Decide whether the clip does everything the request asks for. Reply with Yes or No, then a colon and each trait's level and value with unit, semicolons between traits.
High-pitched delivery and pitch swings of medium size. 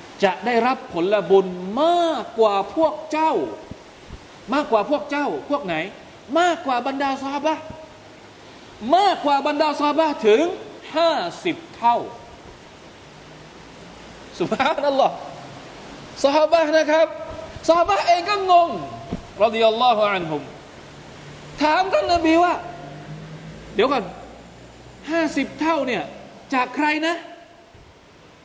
No: very high, 300 Hz; wide, 5.8 semitones